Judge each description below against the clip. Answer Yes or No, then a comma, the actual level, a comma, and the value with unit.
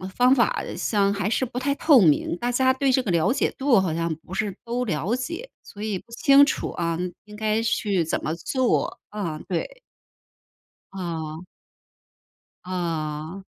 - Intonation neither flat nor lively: No, wide, 6.8 semitones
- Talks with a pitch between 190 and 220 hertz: Yes, high, 205 Hz